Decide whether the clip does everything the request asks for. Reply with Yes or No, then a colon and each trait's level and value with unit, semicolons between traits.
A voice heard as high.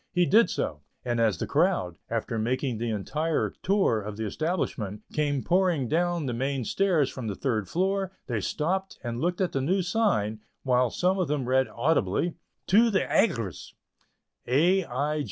No: low, 135 Hz